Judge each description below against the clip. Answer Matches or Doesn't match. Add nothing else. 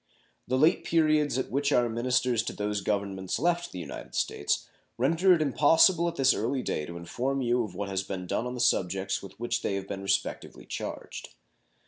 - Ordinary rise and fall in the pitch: Doesn't match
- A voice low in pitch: Matches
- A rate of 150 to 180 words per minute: Doesn't match